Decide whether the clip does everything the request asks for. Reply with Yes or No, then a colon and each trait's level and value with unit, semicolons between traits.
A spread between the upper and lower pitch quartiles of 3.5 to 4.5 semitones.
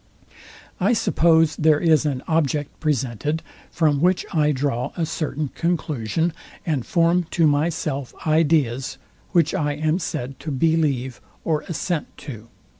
No: average, 2.9 semitones